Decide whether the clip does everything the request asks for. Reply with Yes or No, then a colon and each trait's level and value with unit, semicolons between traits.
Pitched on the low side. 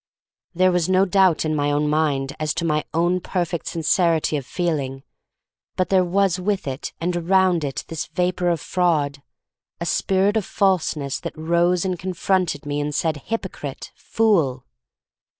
No: medium, 170 Hz